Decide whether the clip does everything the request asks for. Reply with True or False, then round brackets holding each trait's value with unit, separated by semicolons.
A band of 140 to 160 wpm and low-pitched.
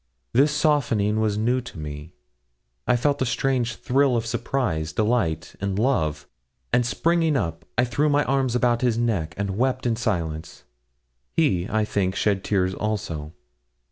True (155 wpm; 115 Hz)